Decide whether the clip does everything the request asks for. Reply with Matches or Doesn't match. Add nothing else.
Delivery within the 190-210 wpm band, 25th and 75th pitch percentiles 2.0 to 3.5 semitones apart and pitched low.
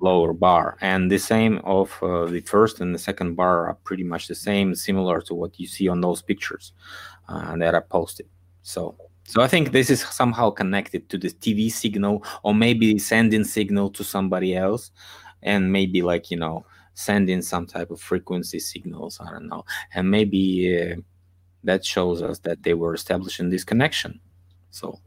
Doesn't match